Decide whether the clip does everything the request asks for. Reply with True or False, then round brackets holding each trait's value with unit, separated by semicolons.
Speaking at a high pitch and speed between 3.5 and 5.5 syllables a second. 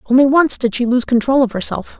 False (255 Hz; 5.9 syllables/s)